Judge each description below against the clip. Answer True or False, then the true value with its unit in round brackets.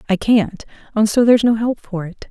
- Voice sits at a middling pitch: False (215 Hz)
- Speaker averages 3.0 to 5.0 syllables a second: False (5.4 syllables/s)